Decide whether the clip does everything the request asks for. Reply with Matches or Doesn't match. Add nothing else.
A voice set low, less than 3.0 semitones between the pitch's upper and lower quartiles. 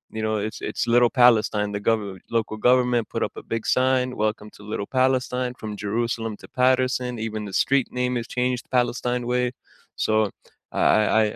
Matches